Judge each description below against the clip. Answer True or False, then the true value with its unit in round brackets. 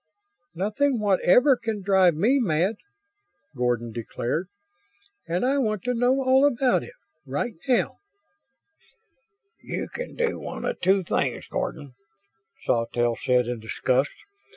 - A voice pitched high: True (195 Hz)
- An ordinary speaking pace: False (125 wpm)